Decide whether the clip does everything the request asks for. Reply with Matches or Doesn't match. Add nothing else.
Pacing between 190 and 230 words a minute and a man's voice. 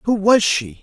Matches